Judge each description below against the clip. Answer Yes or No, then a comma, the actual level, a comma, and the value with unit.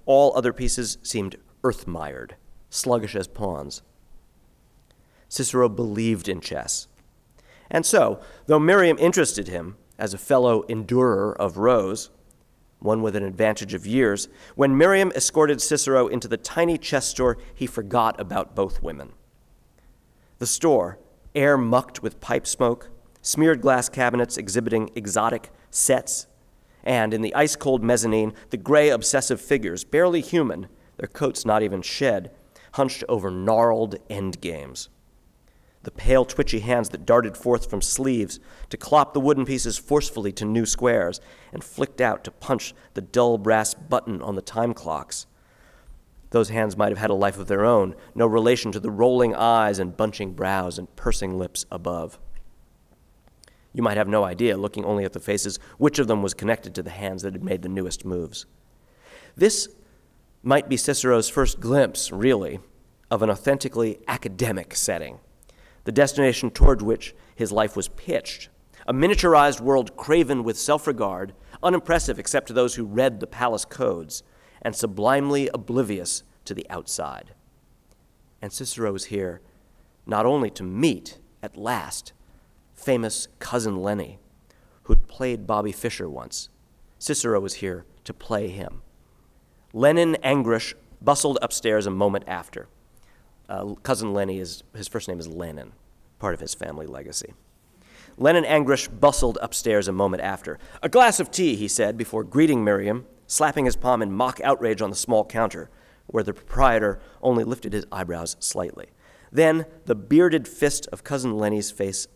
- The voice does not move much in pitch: No, average, 4.6 semitones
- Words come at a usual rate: Yes, average, 155 wpm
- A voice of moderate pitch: No, low, 115 Hz